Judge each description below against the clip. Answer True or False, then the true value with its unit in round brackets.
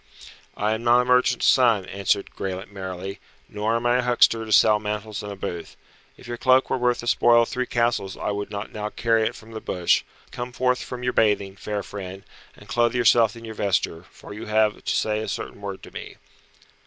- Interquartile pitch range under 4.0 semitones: True (2.9 semitones)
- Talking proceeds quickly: True (220 wpm)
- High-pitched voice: False (110 Hz)